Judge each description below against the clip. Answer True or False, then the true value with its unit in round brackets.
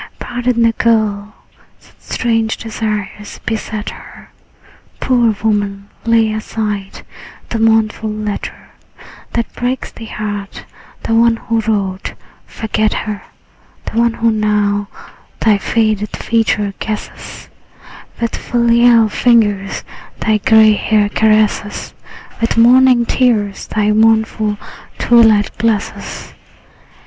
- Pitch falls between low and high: False (220 Hz)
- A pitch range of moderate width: False (1.6 semitones)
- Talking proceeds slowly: True (105 wpm)